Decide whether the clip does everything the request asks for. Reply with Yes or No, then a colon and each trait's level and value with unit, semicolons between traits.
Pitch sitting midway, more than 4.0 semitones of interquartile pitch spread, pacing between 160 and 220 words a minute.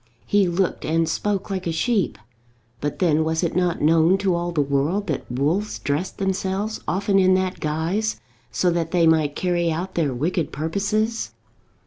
No: medium, 175 Hz; average, 3.3 semitones; average, 170 wpm